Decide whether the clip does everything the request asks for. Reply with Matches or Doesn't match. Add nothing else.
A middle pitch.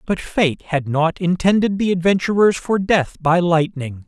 Matches